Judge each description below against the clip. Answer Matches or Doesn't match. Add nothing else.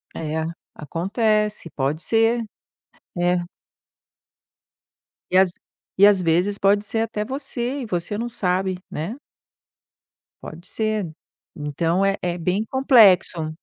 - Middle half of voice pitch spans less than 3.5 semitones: Doesn't match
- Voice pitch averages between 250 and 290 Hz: Doesn't match